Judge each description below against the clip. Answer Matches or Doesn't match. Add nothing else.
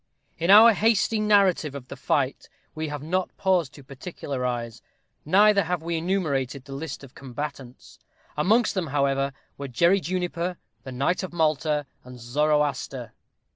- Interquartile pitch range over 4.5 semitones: Matches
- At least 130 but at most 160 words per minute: Matches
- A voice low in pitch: Doesn't match